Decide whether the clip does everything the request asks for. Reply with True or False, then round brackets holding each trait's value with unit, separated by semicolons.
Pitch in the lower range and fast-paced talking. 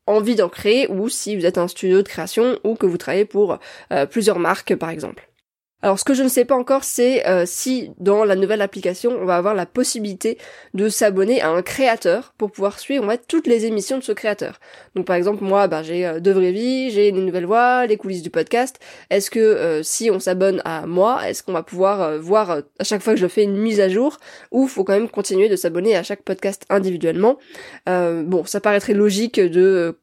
False (200 Hz; 230 wpm)